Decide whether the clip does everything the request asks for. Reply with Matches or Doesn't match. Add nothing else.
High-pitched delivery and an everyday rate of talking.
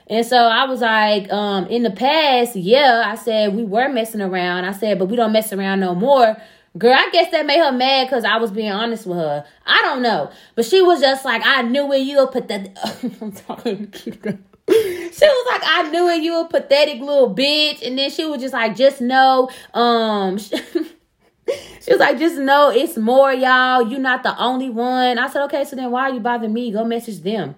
Doesn't match